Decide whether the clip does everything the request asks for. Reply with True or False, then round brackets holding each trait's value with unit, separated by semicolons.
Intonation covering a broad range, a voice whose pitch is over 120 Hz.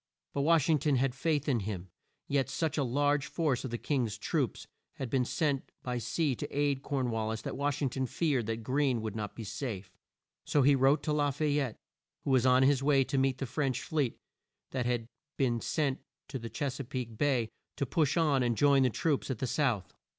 False (3.1 semitones; 135 Hz)